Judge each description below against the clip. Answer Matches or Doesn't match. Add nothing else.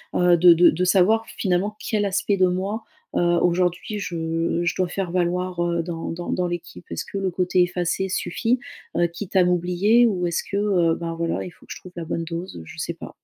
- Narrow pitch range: Matches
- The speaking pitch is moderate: Matches